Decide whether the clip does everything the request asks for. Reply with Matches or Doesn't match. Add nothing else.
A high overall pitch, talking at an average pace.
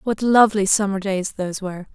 Matches